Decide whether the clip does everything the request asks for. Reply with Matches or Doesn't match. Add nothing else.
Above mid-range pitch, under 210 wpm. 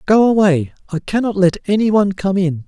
Matches